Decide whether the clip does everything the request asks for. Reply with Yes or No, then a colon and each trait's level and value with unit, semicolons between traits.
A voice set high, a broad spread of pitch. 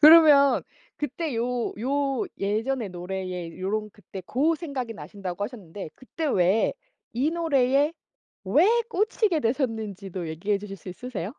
Yes: high, 235 Hz; wide, 6.6 semitones